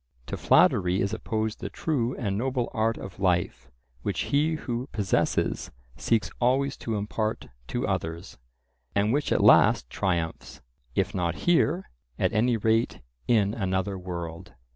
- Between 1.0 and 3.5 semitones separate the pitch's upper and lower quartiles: No, average, 4.4 semitones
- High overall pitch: No, low, 110 Hz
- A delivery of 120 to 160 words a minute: Yes, average, 140 wpm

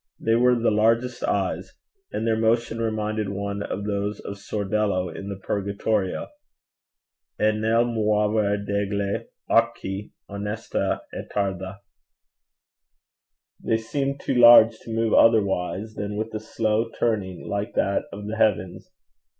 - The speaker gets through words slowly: Yes, slow, 130 wpm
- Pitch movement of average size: No, narrow, 1.9 semitones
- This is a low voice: Yes, low, 105 Hz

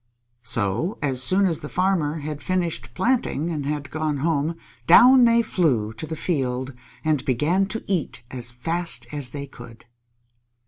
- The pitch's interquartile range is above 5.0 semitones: Yes, wide, 5.4 semitones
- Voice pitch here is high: No, medium, 150 Hz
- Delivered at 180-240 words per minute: No, average, 155 wpm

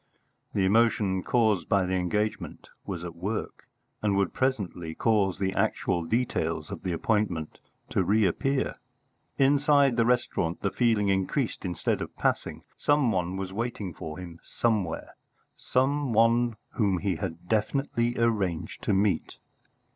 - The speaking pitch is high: No, low, 105 Hz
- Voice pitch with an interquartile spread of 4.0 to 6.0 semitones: Yes, average, 4.3 semitones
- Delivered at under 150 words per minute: Yes, average, 140 wpm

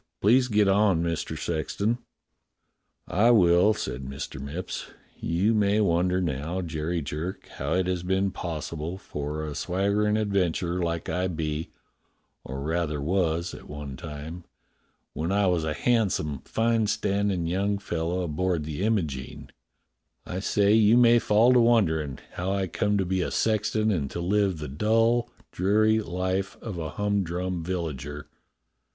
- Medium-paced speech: Yes, average, 150 wpm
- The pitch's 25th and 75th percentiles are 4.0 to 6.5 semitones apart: Yes, average, 4.3 semitones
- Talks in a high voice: No, very low, 90 Hz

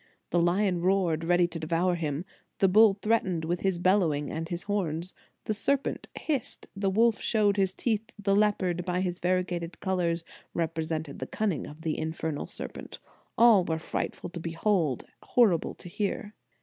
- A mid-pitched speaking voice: Yes, medium, 180 Hz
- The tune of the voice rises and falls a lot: No, average, 3.4 semitones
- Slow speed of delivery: No, average, 165 wpm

